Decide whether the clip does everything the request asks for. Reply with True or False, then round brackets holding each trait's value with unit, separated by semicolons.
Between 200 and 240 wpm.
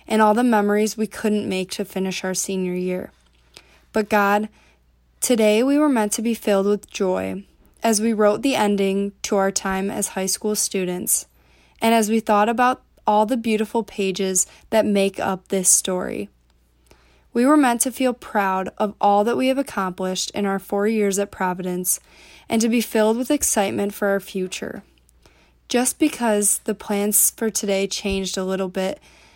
False (175 wpm)